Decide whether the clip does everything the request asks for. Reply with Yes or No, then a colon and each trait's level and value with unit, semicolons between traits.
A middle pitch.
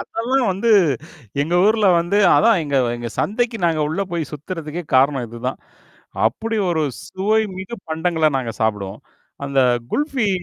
Yes: medium, 170 Hz